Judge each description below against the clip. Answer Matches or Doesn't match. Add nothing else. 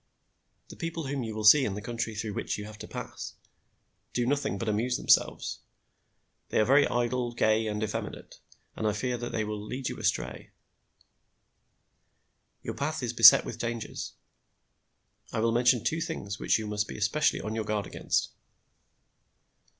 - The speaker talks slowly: Doesn't match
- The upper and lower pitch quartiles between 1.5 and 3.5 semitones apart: Matches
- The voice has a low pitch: Matches